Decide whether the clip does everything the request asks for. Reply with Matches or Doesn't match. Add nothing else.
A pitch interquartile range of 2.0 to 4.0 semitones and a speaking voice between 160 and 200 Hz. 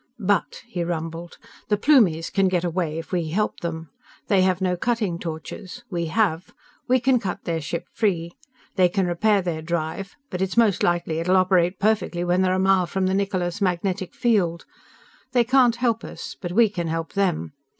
Matches